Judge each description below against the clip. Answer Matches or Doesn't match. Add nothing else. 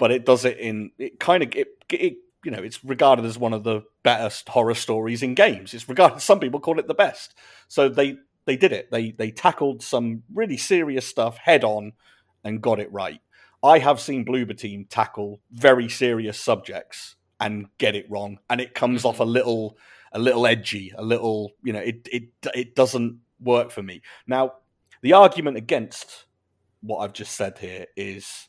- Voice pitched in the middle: Doesn't match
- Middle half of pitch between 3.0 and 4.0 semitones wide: Matches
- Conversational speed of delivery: Matches